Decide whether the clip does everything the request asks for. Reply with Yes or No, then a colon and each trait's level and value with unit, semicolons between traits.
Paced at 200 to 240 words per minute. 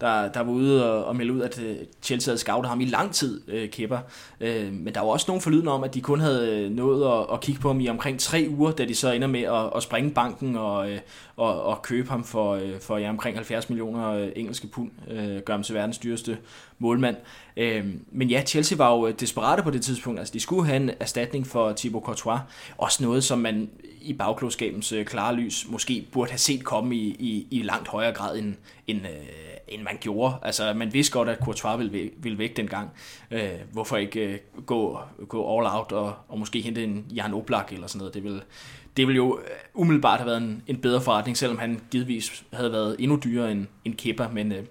Yes: average, 220 wpm